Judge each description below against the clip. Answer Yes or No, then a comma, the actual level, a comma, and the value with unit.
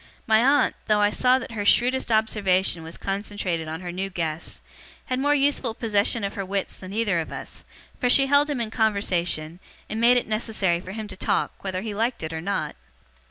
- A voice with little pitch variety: No, average, 4.1 semitones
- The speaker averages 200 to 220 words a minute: Yes, fast, 205 wpm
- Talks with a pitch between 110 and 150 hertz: No, high, 205 Hz